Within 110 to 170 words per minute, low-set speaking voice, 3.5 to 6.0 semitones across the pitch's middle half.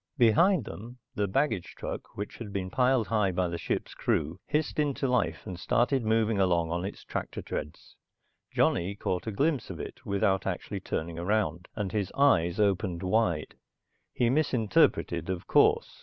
Yes: average, 165 wpm; low, 100 Hz; average, 5.1 semitones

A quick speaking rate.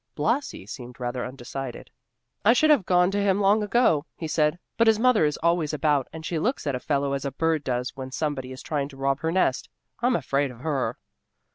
Yes: fast, 220 wpm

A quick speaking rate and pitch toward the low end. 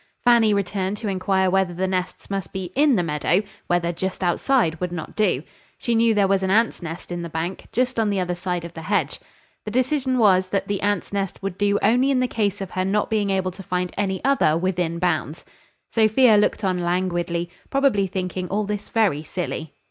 No: fast, 210 wpm; high, 190 Hz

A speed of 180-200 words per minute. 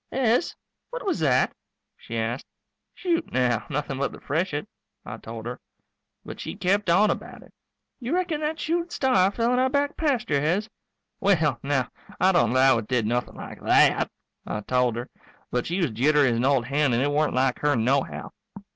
Yes: average, 190 wpm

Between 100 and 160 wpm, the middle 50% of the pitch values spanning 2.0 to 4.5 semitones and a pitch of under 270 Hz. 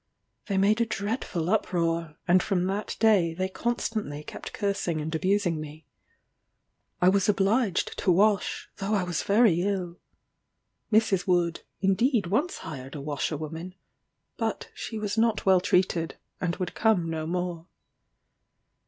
Yes: average, 140 wpm; average, 3.7 semitones; medium, 185 Hz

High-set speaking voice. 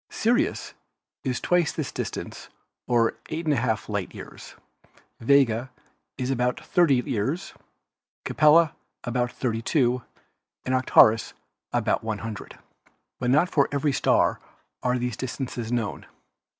No: low, 125 Hz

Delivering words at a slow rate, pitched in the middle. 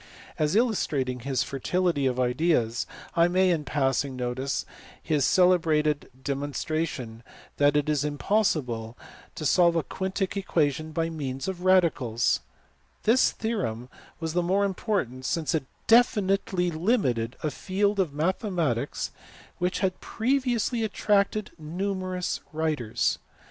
Yes: slow, 125 wpm; medium, 160 Hz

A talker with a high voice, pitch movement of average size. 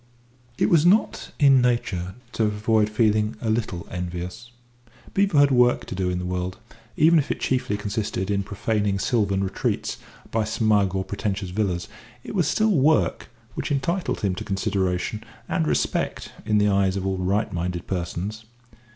No: low, 105 Hz; average, 4.1 semitones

